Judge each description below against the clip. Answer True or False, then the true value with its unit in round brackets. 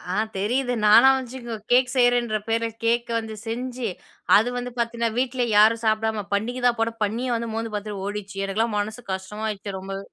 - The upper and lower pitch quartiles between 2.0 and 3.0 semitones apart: True (2.7 semitones)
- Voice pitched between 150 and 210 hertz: False (225 Hz)